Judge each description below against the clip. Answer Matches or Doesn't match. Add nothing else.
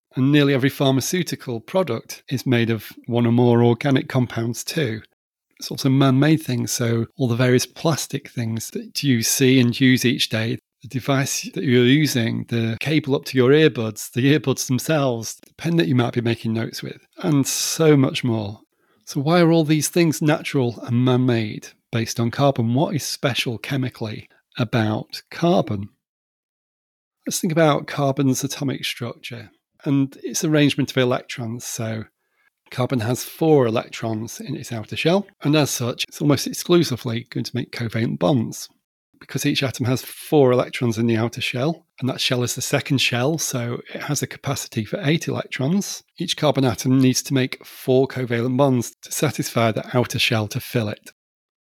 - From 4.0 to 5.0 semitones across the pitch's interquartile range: Doesn't match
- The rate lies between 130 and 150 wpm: Doesn't match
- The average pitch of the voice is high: Doesn't match